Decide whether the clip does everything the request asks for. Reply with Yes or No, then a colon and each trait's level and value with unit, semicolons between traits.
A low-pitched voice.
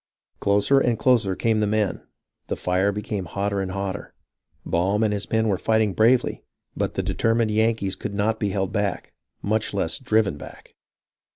Yes: low, 105 Hz